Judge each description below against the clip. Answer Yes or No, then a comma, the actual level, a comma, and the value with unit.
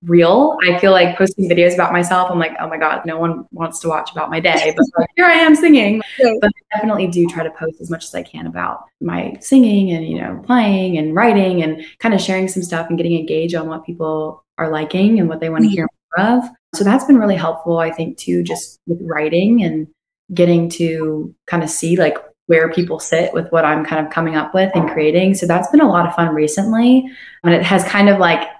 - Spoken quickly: Yes, fast, 240 wpm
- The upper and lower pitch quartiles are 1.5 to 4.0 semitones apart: Yes, average, 3.4 semitones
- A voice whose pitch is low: No, medium, 170 Hz